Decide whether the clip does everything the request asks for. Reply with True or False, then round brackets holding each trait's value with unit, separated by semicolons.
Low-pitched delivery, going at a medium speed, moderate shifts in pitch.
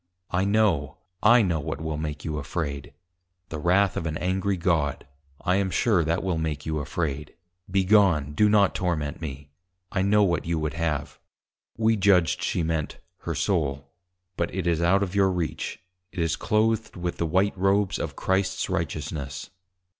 True (85 Hz; 175 wpm; 4.1 semitones)